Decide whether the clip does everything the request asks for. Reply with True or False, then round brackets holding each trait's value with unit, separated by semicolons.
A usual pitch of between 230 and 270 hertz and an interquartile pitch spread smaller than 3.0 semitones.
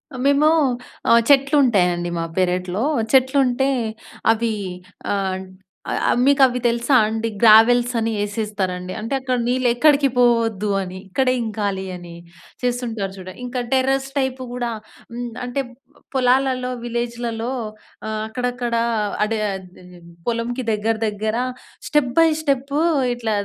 False (235 Hz; 3.3 semitones)